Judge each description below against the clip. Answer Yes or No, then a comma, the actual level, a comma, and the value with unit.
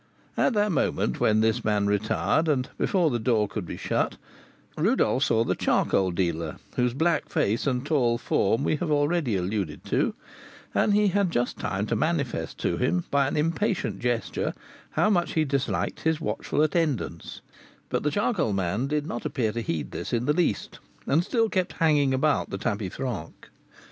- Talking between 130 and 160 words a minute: No, average, 180 wpm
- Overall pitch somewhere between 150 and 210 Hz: No, low, 135 Hz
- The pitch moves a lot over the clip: Yes, wide, 7.0 semitones